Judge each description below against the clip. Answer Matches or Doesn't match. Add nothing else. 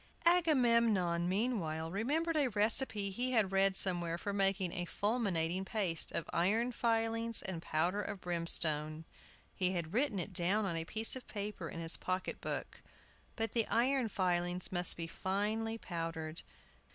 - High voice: Matches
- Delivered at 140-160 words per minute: Matches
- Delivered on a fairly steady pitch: Doesn't match